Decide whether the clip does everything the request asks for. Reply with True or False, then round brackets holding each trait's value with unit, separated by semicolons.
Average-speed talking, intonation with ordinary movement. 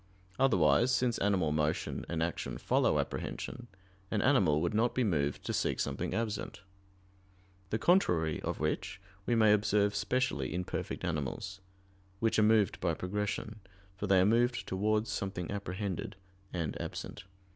True (145 wpm; 4.1 semitones)